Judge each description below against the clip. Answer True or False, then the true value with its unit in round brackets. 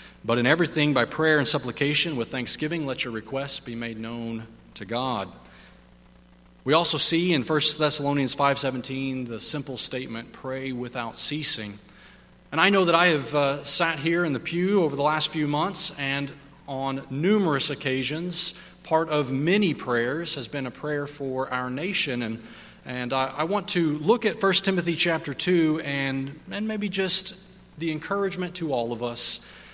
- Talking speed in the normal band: True (170 wpm)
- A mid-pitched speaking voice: True (145 Hz)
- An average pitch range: True (4.6 semitones)